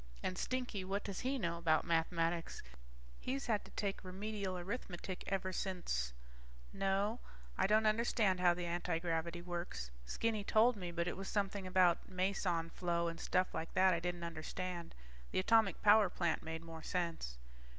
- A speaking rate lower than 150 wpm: No, average, 165 wpm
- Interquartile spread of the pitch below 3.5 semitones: Yes, average, 2.9 semitones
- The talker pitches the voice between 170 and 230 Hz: Yes, medium, 185 Hz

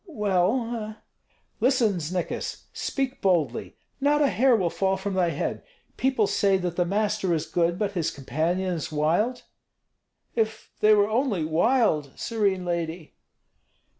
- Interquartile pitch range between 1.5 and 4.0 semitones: No, average, 4.6 semitones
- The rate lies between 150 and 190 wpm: No, slow, 135 wpm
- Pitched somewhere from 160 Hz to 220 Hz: Yes, high, 190 Hz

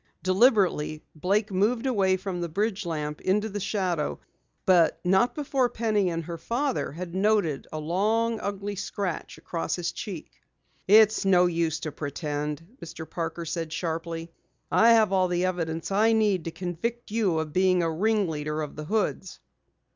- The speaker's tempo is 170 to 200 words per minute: No, average, 160 wpm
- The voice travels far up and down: No, average, 4.2 semitones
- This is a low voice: No, medium, 185 Hz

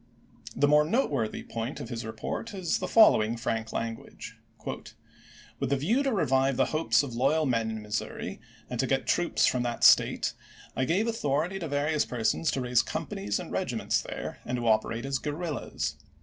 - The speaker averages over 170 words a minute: Yes, average, 180 wpm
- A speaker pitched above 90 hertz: Yes, low, 135 Hz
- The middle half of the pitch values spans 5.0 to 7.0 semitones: Yes, wide, 5.4 semitones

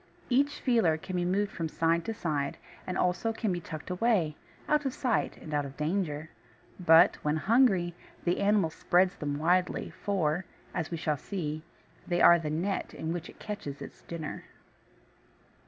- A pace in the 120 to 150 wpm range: No, average, 170 wpm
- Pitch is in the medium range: Yes, medium, 175 Hz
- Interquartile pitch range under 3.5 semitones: No, average, 4.2 semitones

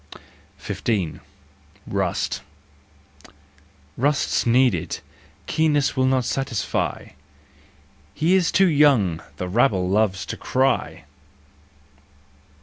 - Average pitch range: No, wide, 6.7 semitones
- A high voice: No, low, 130 Hz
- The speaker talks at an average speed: No, slow, 90 wpm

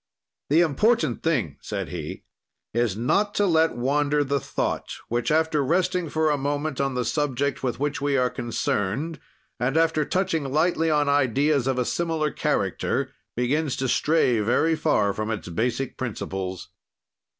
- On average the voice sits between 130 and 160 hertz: Yes, medium, 140 Hz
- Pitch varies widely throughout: No, average, 4.3 semitones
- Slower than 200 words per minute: Yes, average, 155 wpm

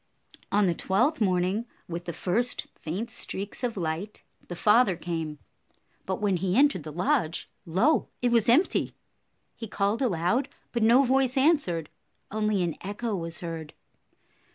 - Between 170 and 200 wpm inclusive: No, average, 150 wpm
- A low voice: No, high, 200 Hz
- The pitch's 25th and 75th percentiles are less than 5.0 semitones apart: No, wide, 5.6 semitones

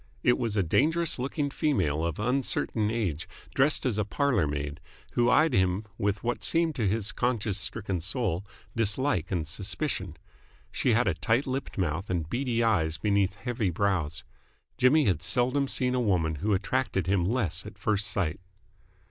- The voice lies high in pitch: No, low, 105 Hz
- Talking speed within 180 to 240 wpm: No, average, 165 wpm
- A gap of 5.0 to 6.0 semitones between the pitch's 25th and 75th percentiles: Yes, wide, 5.6 semitones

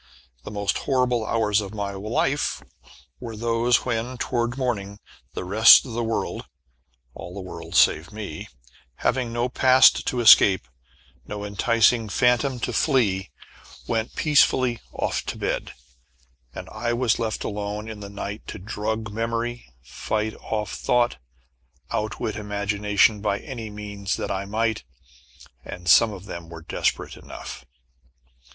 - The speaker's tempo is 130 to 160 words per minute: Yes, average, 140 wpm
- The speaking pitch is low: Yes, low, 110 Hz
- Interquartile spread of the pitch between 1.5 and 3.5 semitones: Yes, average, 2.7 semitones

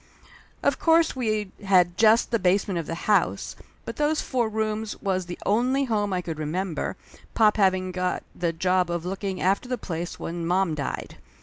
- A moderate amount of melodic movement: Yes, average, 3.6 semitones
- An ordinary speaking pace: Yes, average, 180 wpm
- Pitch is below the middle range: No, high, 190 Hz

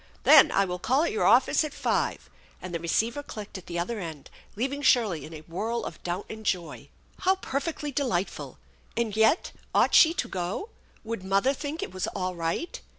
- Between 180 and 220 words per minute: Yes, average, 200 wpm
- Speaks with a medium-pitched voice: No, high, 220 Hz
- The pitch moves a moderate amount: No, wide, 7.8 semitones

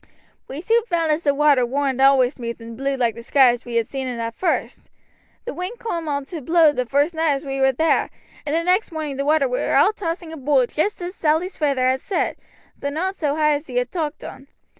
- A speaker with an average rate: No, fast, 240 wpm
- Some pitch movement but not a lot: Yes, average, 3.8 semitones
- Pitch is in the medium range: No, very high, 290 Hz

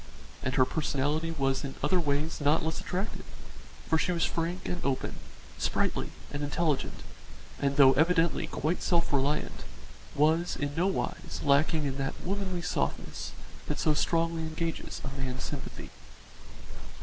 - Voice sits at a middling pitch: Yes, medium, 155 Hz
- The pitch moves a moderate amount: Yes, average, 3.1 semitones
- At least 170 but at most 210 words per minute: No, average, 140 wpm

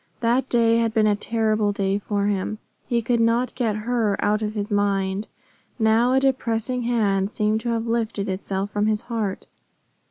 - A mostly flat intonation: Yes, narrow, 2.3 semitones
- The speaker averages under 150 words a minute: No, average, 180 wpm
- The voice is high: Yes, high, 220 Hz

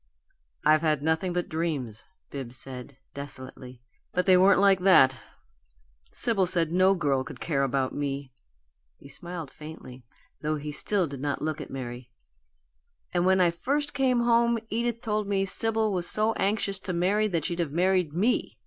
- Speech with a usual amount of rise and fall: No, wide, 5.7 semitones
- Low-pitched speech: No, medium, 170 Hz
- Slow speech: No, average, 165 wpm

